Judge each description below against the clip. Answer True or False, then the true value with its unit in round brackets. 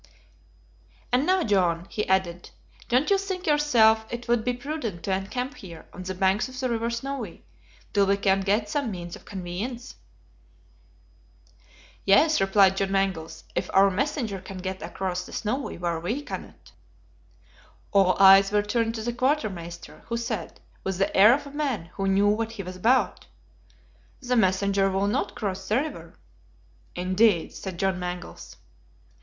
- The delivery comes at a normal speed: True (160 wpm)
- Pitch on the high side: True (200 Hz)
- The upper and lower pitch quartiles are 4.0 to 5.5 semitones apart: True (4.3 semitones)